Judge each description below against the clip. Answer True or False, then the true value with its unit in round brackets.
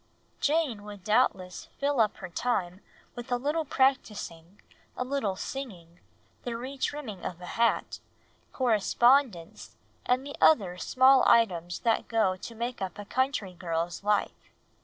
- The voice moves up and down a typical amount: False (5.8 semitones)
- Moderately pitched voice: False (225 Hz)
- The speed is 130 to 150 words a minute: True (140 wpm)